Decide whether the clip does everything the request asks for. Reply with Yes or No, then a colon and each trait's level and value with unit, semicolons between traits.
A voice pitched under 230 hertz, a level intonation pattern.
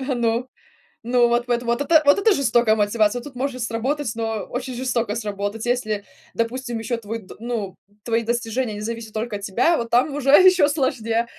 No: high, 235 Hz; narrow, 2.3 semitones